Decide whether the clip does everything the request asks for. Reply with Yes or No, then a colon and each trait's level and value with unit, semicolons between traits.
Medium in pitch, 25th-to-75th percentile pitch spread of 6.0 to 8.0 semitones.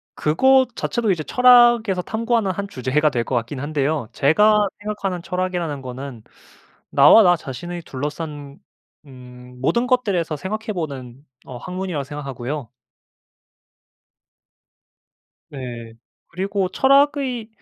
Yes: medium, 160 Hz; wide, 7.0 semitones